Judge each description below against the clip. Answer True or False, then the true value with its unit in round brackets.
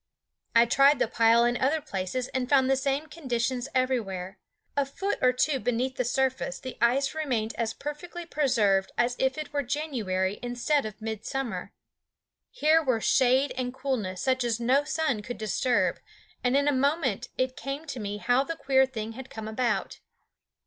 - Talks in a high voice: True (255 Hz)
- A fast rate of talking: False (175 wpm)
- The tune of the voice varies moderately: True (3.2 semitones)